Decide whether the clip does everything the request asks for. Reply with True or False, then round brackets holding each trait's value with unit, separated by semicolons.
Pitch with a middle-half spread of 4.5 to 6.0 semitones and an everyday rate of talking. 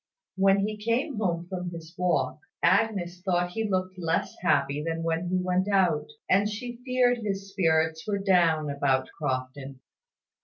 False (3.7 semitones; 155 wpm)